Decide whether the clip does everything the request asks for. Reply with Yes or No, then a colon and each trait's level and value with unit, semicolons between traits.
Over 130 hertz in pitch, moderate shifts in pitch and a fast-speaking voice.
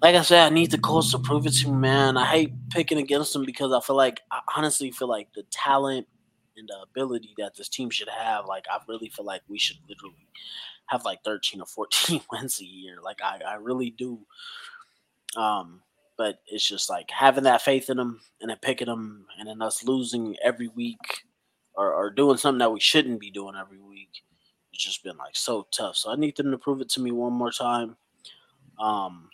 No: low, 125 Hz; average, 3.7 semitones; fast, 220 wpm